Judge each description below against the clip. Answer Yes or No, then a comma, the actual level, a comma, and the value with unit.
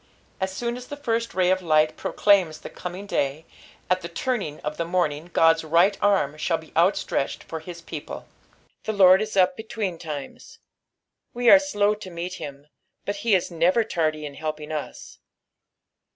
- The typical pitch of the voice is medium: Yes, medium, 180 Hz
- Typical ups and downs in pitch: Yes, average, 4.5 semitones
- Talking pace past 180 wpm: No, average, 170 wpm